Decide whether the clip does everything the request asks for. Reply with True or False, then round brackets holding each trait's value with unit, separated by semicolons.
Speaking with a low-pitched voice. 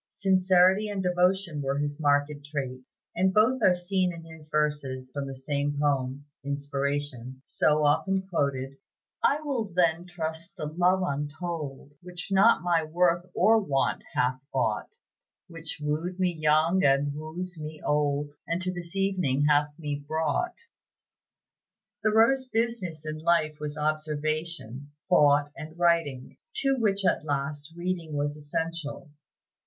False (155 Hz)